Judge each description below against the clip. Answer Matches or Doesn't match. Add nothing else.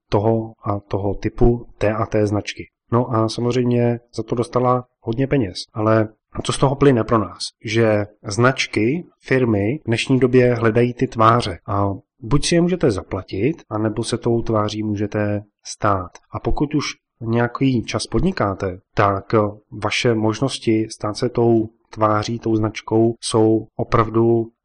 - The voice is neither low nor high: Doesn't match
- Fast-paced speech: Doesn't match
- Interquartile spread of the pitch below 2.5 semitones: Matches